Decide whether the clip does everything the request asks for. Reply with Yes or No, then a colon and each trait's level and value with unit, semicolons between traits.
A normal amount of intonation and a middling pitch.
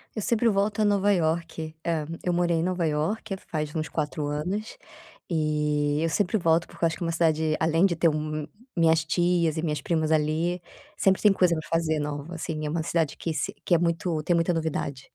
No: narrow, 2.2 semitones; medium, 165 Hz